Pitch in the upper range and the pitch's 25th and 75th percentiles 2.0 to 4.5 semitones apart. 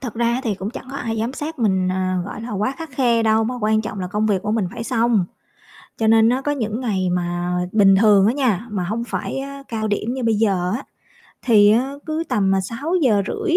Yes: high, 220 Hz; average, 4.0 semitones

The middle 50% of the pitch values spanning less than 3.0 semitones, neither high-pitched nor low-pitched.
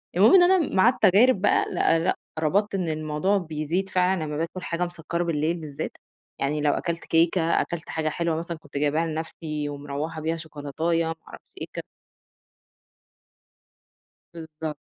Yes: narrow, 2.6 semitones; medium, 165 Hz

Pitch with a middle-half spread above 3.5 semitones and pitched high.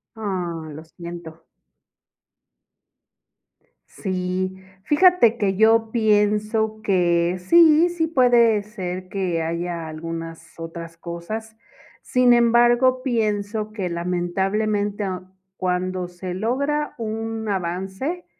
Yes: average, 4.2 semitones; high, 205 Hz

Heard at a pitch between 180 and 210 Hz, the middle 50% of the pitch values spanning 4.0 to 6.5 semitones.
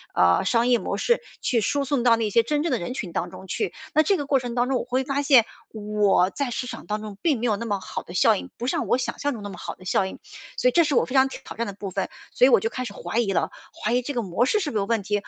No: high, 235 Hz; average, 4.5 semitones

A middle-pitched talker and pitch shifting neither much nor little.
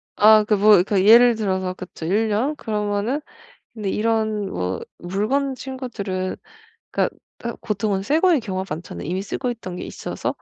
No: high, 210 Hz; average, 3.5 semitones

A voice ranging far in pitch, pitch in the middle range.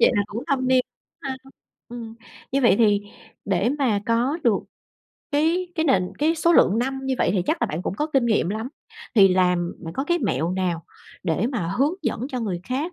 No: wide, 6.0 semitones; high, 235 Hz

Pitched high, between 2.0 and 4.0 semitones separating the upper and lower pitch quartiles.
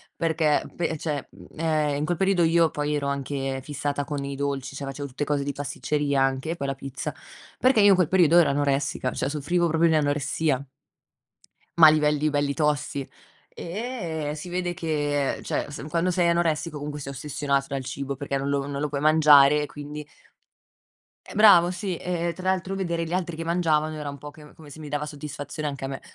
No: medium, 150 Hz; average, 2.9 semitones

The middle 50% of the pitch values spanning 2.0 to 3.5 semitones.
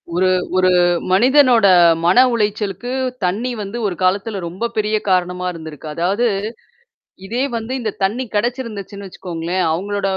No: average, 3.9 semitones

